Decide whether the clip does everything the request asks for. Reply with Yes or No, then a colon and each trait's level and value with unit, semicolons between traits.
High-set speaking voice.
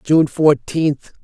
No: medium, 150 Hz